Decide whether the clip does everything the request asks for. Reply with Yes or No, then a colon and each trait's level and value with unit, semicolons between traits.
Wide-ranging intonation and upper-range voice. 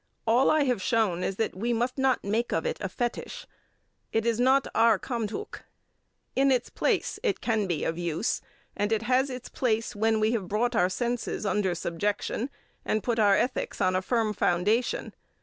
No: average, 3.3 semitones; high, 225 Hz